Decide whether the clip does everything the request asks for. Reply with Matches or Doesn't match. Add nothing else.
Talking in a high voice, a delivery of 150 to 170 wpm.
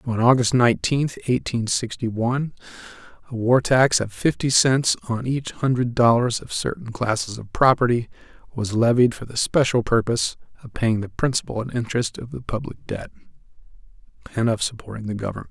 Doesn't match